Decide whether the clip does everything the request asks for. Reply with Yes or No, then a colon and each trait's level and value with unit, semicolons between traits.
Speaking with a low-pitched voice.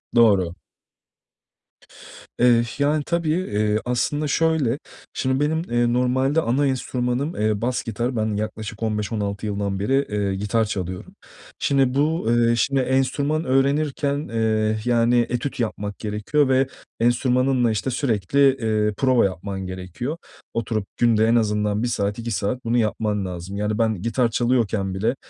Yes: low, 115 Hz